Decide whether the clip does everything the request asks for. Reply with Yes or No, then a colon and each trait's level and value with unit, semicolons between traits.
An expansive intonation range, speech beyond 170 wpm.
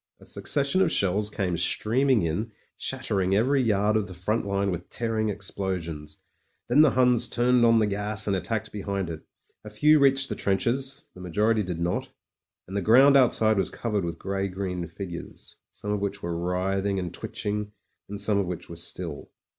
No: average, 3.8 semitones; average, 190 wpm